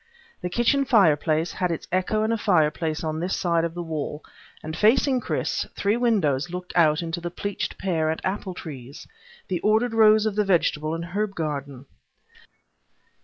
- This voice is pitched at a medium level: Yes, medium, 175 Hz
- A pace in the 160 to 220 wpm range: Yes, average, 170 wpm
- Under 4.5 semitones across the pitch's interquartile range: No, average, 5.0 semitones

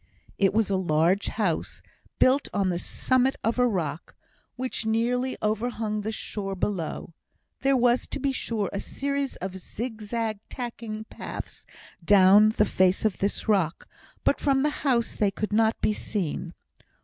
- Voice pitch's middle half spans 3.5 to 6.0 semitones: Yes, average, 4.0 semitones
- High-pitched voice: Yes, high, 215 Hz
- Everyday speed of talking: Yes, average, 155 wpm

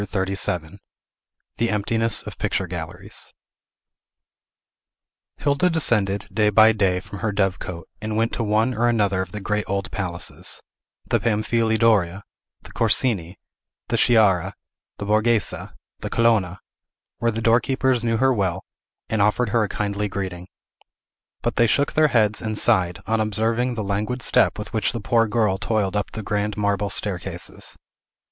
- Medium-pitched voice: No, low, 105 Hz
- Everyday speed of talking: Yes, average, 155 wpm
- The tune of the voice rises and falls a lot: No, average, 2.7 semitones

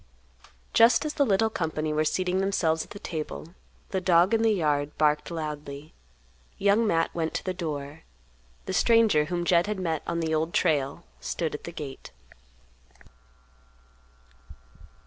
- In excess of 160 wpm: No, average, 150 wpm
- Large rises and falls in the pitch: No, average, 3.8 semitones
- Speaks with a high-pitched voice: No, medium, 170 Hz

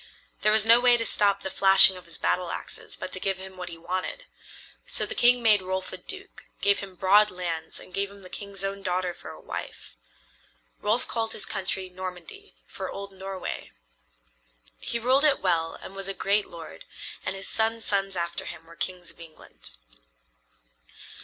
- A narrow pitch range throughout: Yes, narrow, 2.3 semitones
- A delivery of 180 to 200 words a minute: Yes, average, 185 wpm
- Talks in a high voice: Yes, high, 195 Hz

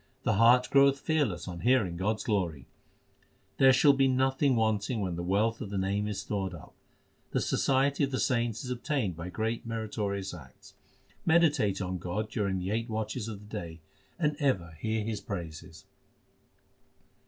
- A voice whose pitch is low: Yes, low, 110 Hz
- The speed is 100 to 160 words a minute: No, average, 170 wpm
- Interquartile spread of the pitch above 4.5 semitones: Yes, average, 5.1 semitones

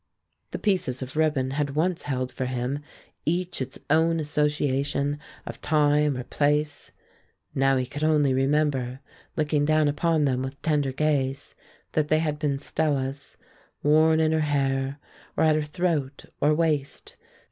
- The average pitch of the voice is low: No, medium, 145 Hz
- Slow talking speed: No, average, 150 wpm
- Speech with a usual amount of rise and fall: No, narrow, 2.3 semitones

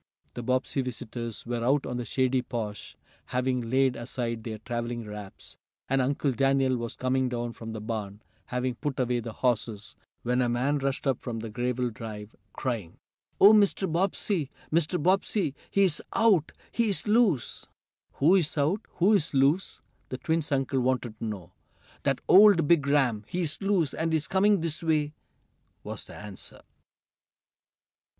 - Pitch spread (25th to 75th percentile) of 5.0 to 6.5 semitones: Yes, average, 5.3 semitones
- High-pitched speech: No, low, 130 Hz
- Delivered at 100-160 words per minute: Yes, average, 150 wpm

